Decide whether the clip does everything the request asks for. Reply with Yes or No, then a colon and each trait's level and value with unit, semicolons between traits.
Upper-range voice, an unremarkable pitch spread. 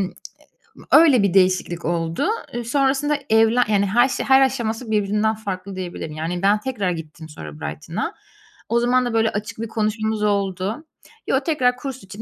Yes: high, 215 Hz; average, 4.9 semitones